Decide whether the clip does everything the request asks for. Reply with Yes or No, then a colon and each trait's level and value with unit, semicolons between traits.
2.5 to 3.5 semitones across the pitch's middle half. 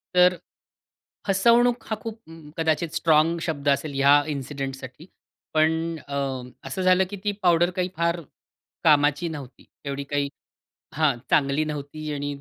No: average, 3.9 semitones